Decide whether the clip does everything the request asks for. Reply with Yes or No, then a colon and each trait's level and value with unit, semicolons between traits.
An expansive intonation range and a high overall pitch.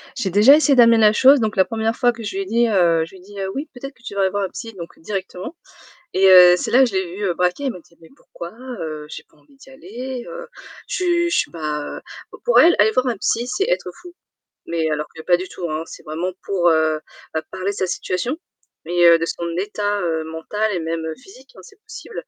Yes: wide, 6.2 semitones; high, 195 Hz